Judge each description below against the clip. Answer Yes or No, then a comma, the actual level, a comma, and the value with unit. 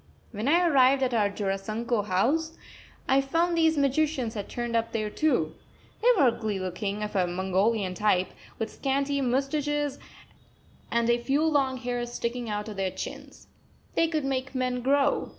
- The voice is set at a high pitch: Yes, high, 245 Hz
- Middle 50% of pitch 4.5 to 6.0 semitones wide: Yes, average, 4.9 semitones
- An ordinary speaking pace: Yes, average, 165 wpm